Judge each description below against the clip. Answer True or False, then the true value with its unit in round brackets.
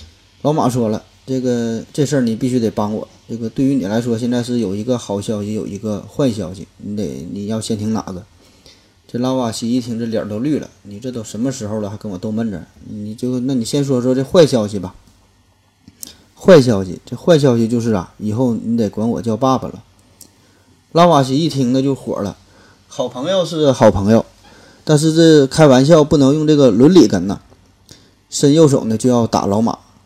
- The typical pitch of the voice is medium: False (115 Hz)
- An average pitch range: True (4.4 semitones)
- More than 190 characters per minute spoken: True (285 characters per minute)